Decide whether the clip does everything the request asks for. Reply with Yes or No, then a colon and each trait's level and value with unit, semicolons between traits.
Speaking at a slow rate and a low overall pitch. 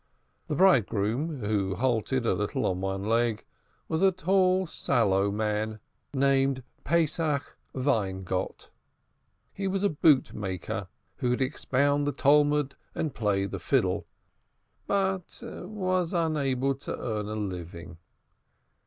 Yes: slow, 120 wpm; low, 130 Hz